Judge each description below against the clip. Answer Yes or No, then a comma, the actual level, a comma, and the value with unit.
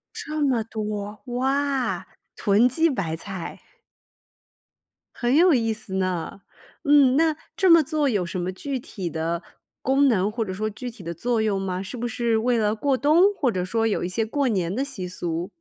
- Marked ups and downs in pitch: Yes, wide, 6.0 semitones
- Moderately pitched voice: No, high, 225 Hz